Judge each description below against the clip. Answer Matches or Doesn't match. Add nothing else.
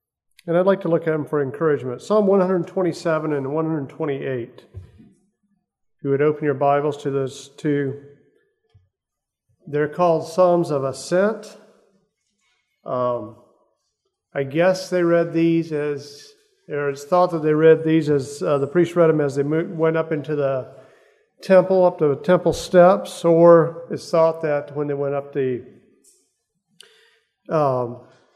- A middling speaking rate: Matches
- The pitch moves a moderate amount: Matches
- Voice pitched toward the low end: Doesn't match